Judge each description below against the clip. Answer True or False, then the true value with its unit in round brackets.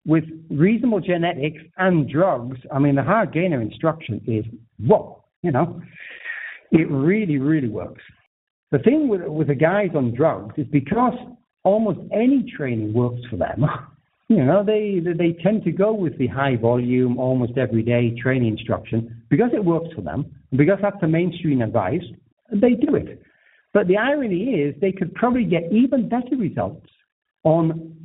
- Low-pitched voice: False (160 Hz)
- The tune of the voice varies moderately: False (7.5 semitones)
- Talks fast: False (165 wpm)